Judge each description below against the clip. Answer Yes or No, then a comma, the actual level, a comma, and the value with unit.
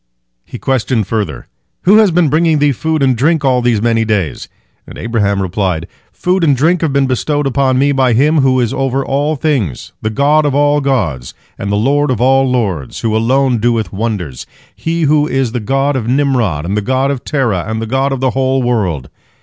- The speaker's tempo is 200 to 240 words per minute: Yes, fast, 205 wpm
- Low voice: Yes, low, 130 Hz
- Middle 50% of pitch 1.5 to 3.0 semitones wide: No, average, 4.4 semitones